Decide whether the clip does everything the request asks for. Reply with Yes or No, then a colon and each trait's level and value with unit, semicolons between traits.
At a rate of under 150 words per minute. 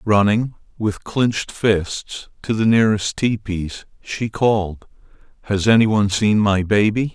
Yes: slow, 135 wpm